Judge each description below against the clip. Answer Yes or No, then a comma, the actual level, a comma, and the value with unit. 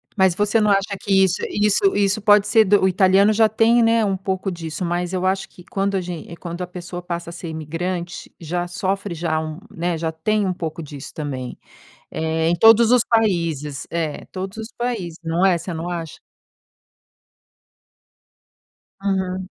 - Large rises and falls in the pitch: No, average, 3.3 semitones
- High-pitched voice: No, medium, 180 Hz